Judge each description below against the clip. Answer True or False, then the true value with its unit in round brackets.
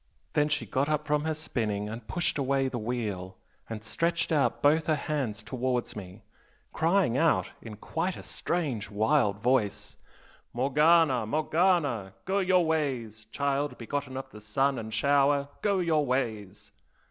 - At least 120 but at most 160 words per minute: True (150 wpm)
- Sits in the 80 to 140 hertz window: True (135 Hz)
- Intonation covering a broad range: True (5.8 semitones)